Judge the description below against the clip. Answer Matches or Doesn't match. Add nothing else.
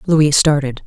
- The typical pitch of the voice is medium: Matches